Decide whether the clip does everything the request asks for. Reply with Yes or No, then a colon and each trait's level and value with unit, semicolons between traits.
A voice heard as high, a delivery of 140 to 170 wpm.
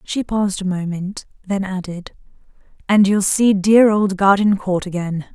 Yes: high, 195 Hz; average, 145 wpm